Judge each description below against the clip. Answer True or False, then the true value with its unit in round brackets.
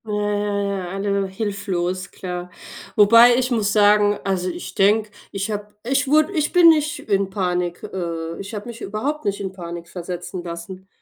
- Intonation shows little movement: False (3.0 semitones)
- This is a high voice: True (200 Hz)